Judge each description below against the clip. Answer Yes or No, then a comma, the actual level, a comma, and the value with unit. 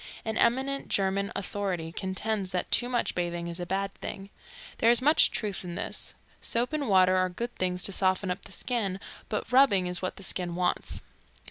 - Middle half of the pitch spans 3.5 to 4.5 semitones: Yes, average, 3.9 semitones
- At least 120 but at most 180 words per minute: No, average, 195 wpm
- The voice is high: Yes, high, 195 Hz